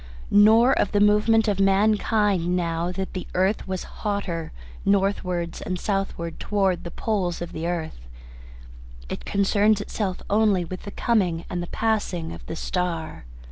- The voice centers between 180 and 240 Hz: Yes, high, 190 Hz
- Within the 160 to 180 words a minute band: No, average, 150 wpm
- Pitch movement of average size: Yes, average, 3.1 semitones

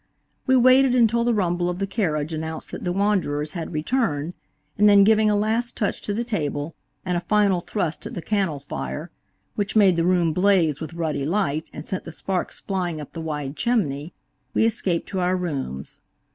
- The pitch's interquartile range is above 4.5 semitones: Yes, average, 5.0 semitones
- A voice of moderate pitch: Yes, medium, 180 Hz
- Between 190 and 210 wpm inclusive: Yes, average, 195 wpm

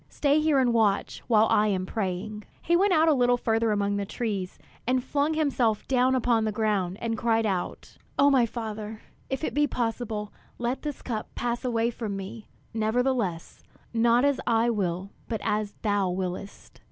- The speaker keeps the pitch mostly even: No, average, 3.2 semitones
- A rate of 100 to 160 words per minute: No, average, 175 wpm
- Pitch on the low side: No, high, 225 Hz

